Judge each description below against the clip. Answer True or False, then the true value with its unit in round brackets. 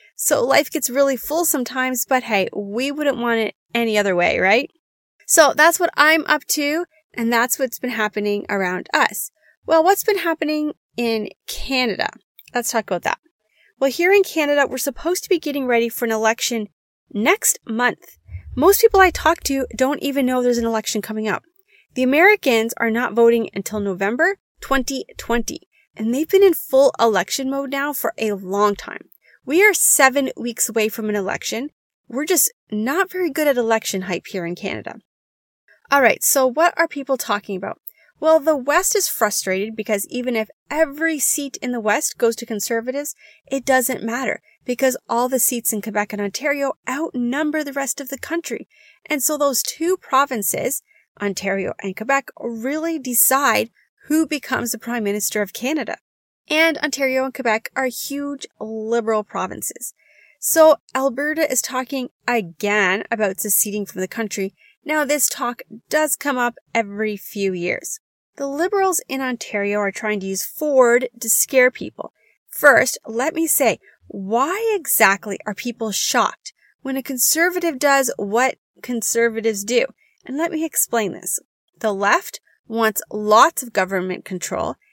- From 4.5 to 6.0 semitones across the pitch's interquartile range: True (5.5 semitones)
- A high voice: True (255 Hz)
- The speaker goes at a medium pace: True (165 wpm)